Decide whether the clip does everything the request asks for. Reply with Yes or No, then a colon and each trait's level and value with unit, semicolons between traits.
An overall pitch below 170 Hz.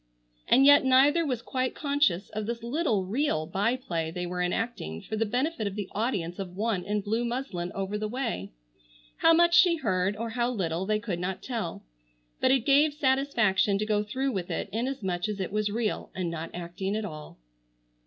No: high, 215 Hz